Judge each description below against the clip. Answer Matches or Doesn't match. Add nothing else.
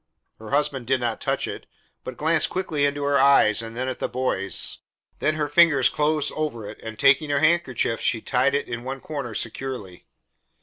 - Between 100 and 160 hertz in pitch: Matches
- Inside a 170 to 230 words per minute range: Matches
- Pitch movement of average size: Matches